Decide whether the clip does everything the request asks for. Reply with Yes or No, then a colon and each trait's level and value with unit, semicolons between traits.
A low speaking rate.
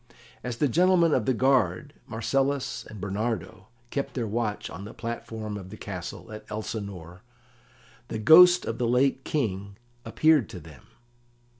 No: average, 150 wpm